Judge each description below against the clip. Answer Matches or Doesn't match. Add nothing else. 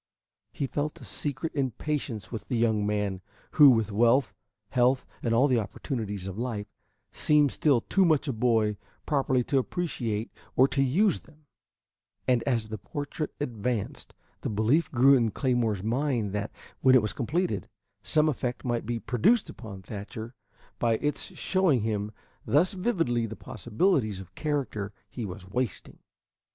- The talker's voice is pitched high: Doesn't match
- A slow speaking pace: Doesn't match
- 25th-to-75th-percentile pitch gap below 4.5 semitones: Doesn't match